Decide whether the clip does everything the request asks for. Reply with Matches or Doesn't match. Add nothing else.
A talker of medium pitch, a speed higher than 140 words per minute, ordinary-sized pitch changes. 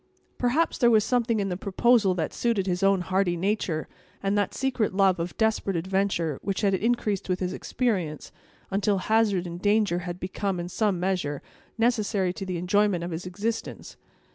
Doesn't match